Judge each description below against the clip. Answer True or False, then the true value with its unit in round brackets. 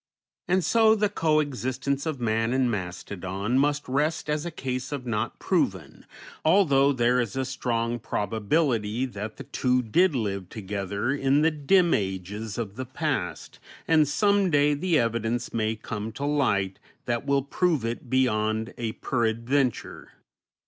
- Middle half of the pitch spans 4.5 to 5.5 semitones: True (5.0 semitones)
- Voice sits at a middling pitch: False (125 Hz)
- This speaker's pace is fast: False (150 wpm)